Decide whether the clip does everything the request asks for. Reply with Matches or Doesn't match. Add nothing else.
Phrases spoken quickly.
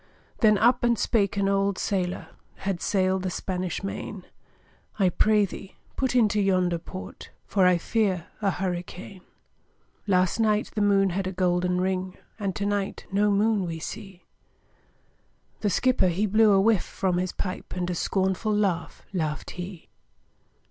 Doesn't match